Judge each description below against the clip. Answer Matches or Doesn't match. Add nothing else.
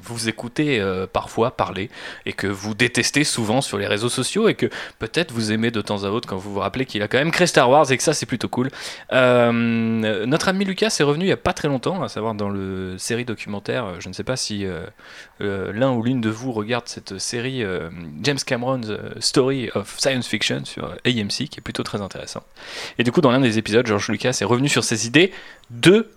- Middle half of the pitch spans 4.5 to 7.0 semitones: Doesn't match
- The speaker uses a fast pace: Matches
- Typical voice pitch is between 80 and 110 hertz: Doesn't match